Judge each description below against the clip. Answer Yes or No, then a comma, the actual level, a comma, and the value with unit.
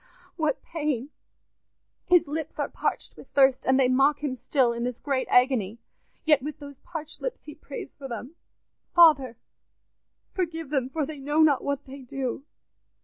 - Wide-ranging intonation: No, average, 2.9 semitones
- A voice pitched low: No, very high, 280 Hz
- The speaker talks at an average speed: Yes, average, 170 wpm